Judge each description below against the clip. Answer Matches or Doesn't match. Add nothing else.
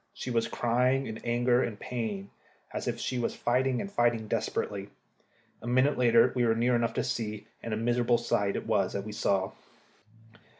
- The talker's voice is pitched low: Matches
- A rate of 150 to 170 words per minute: Doesn't match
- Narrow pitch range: Matches